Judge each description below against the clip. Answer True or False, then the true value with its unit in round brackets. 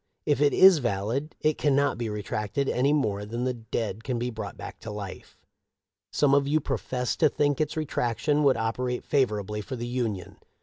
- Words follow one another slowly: False (180 wpm)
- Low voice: True (125 Hz)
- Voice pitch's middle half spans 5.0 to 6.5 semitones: False (4.6 semitones)